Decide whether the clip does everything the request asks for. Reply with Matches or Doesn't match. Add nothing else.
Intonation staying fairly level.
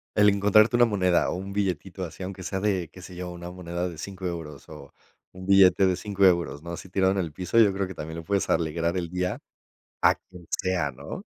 Matches